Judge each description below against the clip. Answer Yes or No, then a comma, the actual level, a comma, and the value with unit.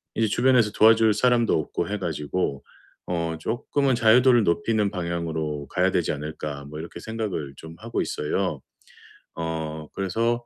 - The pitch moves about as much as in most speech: No, wide, 6.3 semitones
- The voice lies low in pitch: Yes, very low, 90 Hz